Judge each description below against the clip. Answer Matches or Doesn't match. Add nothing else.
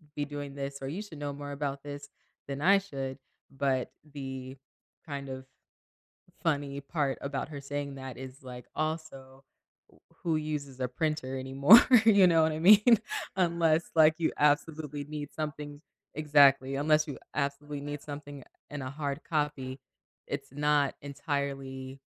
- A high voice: Doesn't match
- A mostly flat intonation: Matches